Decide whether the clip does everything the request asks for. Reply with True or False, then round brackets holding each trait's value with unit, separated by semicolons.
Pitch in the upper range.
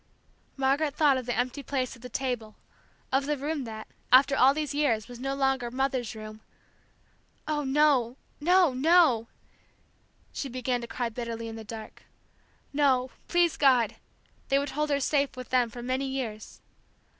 True (260 Hz)